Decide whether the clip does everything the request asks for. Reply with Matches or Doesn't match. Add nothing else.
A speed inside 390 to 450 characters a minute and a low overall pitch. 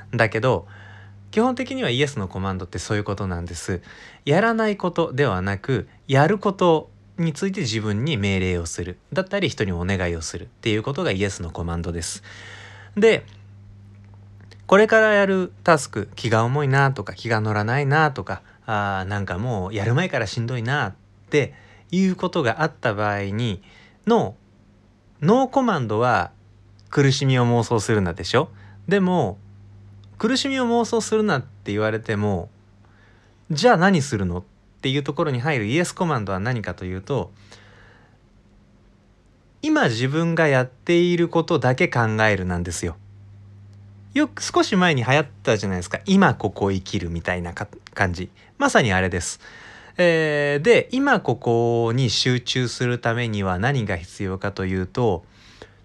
Doesn't match